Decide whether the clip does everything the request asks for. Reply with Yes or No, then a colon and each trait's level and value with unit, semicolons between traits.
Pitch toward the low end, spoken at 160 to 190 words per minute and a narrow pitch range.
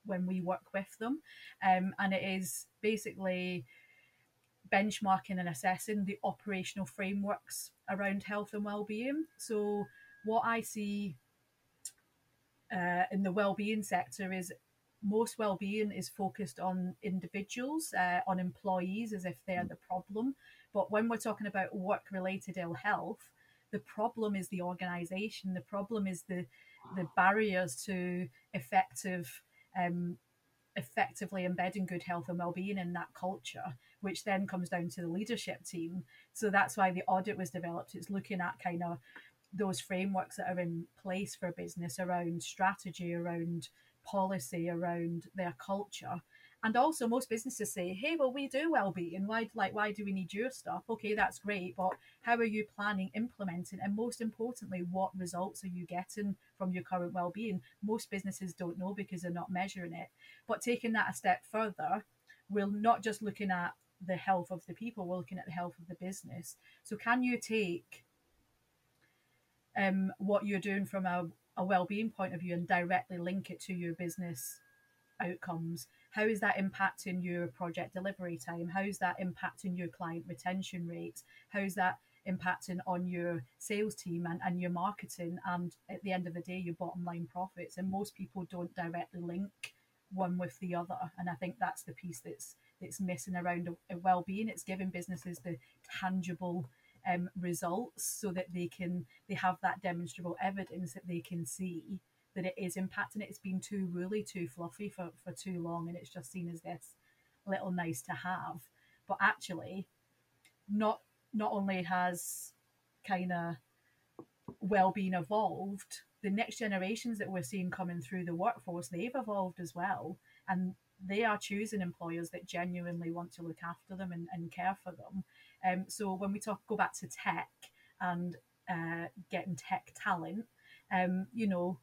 No: medium, 185 Hz; average, 170 wpm; narrow, 2.2 semitones